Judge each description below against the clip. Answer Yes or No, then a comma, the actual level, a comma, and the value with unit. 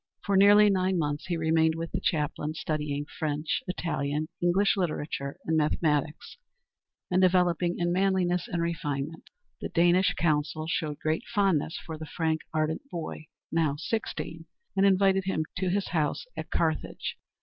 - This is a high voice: No, medium, 165 Hz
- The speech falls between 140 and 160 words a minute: Yes, average, 150 wpm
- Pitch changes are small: No, average, 3.0 semitones